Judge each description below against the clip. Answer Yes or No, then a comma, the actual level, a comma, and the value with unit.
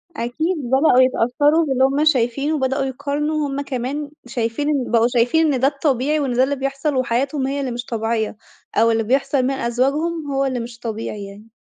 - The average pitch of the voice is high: Yes, very high, 265 Hz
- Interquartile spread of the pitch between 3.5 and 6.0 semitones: No, average, 3.1 semitones